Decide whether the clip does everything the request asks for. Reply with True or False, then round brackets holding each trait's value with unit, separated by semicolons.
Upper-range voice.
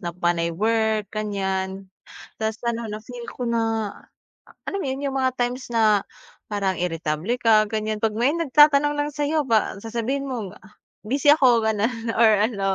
True (225 Hz)